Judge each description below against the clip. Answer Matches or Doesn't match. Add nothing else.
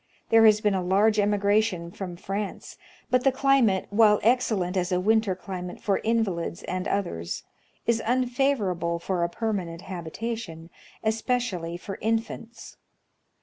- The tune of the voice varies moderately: Matches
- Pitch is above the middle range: Matches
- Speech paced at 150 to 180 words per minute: Doesn't match